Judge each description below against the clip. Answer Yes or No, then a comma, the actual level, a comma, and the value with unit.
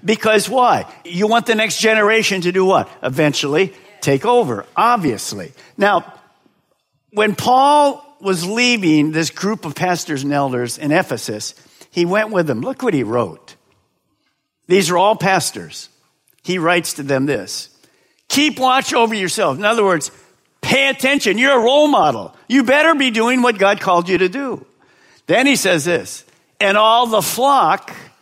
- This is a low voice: No, high, 205 Hz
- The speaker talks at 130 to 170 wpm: Yes, average, 160 wpm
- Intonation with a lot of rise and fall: Yes, wide, 6.1 semitones